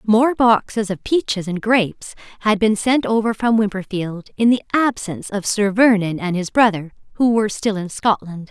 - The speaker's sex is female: Yes, female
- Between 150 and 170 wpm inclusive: No, average, 185 wpm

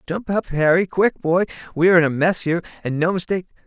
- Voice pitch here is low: No, medium, 175 Hz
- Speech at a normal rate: No, fast, 230 wpm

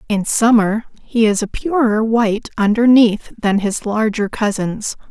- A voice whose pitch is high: Yes, high, 220 Hz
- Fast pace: No, average, 140 wpm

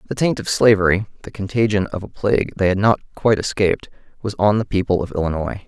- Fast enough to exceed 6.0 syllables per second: Yes, 6.4 syllables/s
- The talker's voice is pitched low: Yes, low, 100 Hz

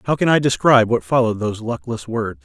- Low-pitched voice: Yes, low, 120 Hz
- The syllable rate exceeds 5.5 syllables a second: Yes, 6.6 syllables/s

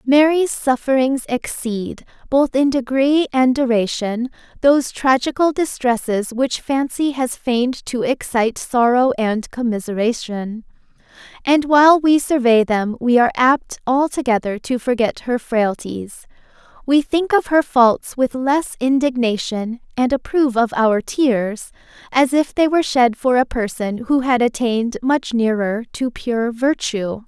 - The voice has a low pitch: No, very high, 250 Hz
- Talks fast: No, slow, 135 wpm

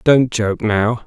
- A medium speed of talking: Yes, average, 170 wpm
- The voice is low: Yes, low, 115 Hz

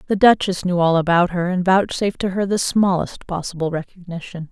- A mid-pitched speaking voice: Yes, medium, 180 Hz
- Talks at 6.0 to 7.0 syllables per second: No, 5.5 syllables/s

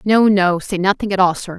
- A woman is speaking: Yes, female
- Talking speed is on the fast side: Yes, fast, 265 wpm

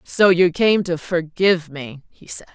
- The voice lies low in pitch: No, medium, 175 Hz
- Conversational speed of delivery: Yes, average, 190 wpm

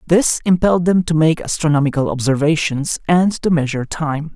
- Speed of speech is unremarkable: Yes, average, 150 wpm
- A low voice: No, medium, 160 Hz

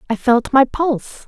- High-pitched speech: Yes, very high, 255 Hz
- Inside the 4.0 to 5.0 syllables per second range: Yes, 4.7 syllables/s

